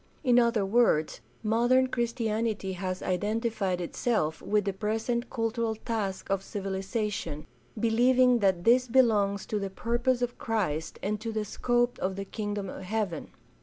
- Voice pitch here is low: No, high, 215 Hz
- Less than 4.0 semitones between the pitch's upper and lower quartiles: Yes, average, 3.5 semitones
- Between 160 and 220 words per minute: No, average, 145 wpm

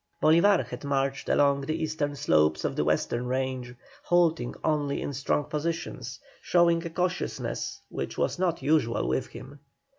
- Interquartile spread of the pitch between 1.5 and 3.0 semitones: No, average, 3.9 semitones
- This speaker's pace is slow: No, average, 150 wpm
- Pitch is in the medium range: Yes, medium, 145 Hz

